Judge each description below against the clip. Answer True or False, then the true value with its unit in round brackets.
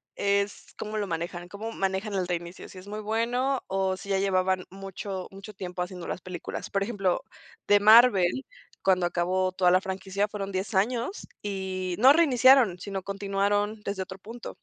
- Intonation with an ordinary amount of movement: False (2.1 semitones)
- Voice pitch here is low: False (195 Hz)